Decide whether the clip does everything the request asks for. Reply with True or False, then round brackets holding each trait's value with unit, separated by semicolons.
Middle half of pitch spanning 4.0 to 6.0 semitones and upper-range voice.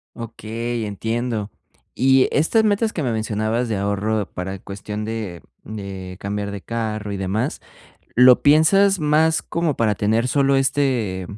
False (4.7 semitones; 115 Hz)